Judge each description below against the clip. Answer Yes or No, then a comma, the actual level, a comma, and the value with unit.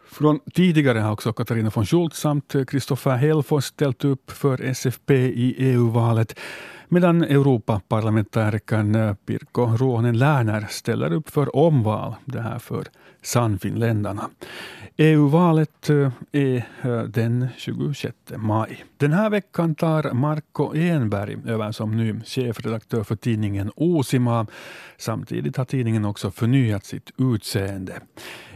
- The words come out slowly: Yes, slow, 115 wpm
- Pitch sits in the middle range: No, low, 125 Hz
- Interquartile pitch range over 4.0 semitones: Yes, average, 4.6 semitones